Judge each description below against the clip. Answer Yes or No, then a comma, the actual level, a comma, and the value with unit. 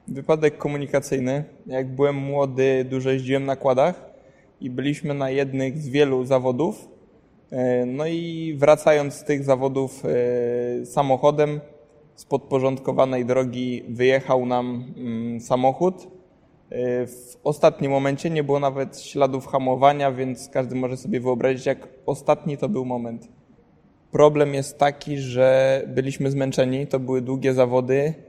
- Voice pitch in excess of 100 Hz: Yes, low, 135 Hz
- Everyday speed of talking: Yes, average, 120 wpm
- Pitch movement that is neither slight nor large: No, narrow, 1.8 semitones